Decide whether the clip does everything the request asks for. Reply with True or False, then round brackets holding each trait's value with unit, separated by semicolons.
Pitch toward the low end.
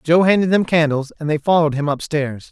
False (155 Hz)